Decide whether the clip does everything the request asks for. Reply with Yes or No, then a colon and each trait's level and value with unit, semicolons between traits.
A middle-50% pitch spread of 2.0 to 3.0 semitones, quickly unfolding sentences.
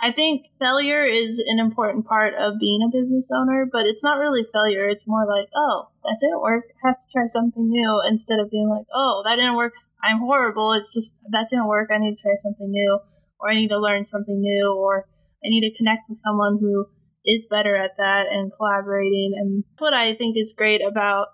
Yes: narrow, 2.5 semitones; fast, 220 wpm